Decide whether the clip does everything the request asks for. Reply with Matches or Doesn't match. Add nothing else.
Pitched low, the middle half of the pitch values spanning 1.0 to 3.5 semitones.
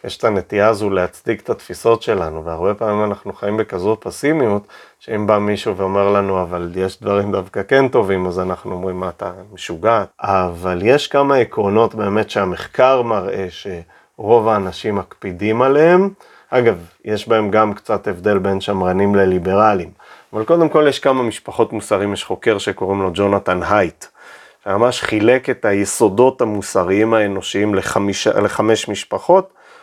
Matches